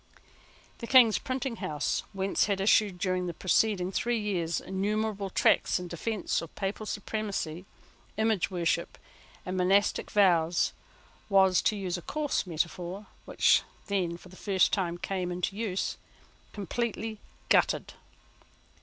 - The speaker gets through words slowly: Yes, slow, 130 wpm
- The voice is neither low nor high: No, high, 195 Hz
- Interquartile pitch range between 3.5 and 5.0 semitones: No, average, 3.0 semitones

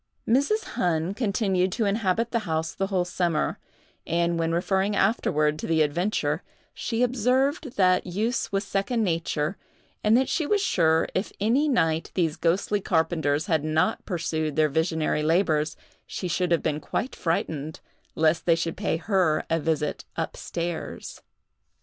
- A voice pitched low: No, medium, 175 Hz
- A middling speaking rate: Yes, average, 155 wpm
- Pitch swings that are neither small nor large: Yes, average, 4.5 semitones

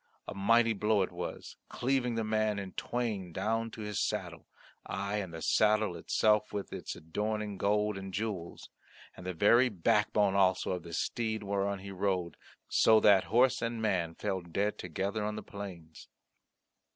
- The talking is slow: No, average, 170 wpm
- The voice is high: No, low, 100 Hz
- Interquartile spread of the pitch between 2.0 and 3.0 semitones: Yes, narrow, 2.5 semitones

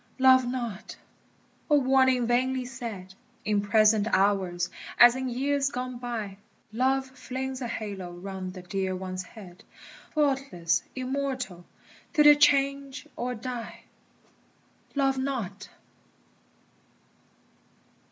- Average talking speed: No, slow, 105 wpm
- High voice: Yes, high, 245 Hz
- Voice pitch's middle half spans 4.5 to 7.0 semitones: Yes, average, 5.1 semitones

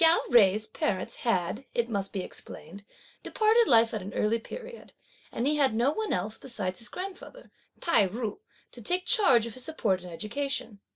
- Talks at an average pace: Yes, average, 180 wpm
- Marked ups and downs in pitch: Yes, wide, 6.9 semitones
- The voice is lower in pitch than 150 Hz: No, high, 230 Hz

